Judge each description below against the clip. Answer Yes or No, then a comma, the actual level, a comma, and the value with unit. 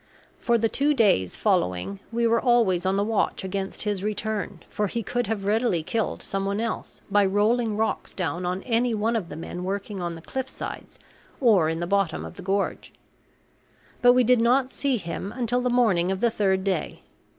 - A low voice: No, high, 205 Hz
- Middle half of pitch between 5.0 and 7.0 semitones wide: No, average, 3.7 semitones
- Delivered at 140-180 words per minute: No, average, 195 wpm